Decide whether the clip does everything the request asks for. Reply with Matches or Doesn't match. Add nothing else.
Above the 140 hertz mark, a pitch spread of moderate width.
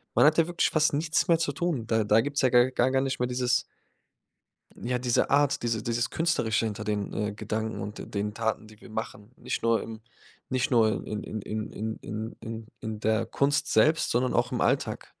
Doesn't match